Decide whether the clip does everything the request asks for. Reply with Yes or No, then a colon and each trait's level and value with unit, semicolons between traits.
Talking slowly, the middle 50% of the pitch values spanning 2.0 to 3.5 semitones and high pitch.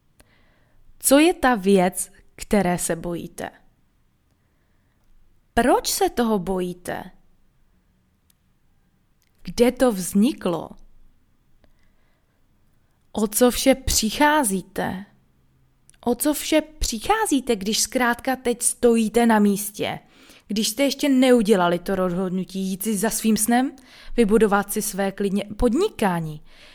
No: slow, 100 wpm; average, 5.1 semitones; high, 220 Hz